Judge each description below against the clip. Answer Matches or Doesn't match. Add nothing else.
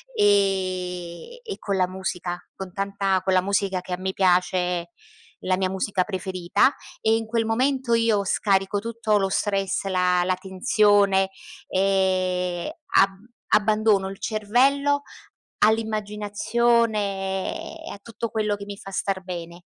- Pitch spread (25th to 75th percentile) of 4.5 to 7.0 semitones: Doesn't match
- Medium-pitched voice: Doesn't match